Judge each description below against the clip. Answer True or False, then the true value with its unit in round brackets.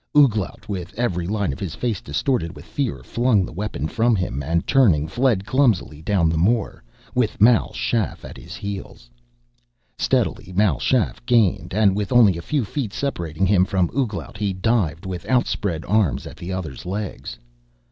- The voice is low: True (100 Hz)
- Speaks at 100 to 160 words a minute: False (170 wpm)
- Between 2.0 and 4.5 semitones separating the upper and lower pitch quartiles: False (5.2 semitones)